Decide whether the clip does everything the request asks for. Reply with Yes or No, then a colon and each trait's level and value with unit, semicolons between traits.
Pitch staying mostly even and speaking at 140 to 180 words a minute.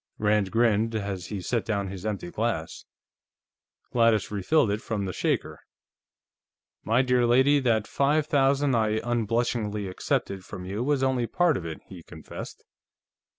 No: average, 3.9 semitones; average, 150 wpm